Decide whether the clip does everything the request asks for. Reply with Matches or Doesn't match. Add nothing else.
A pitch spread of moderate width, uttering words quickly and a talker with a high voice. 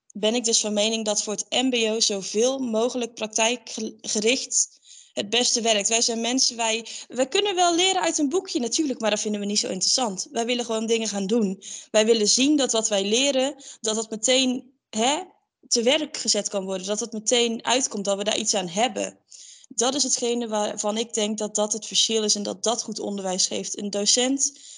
Matches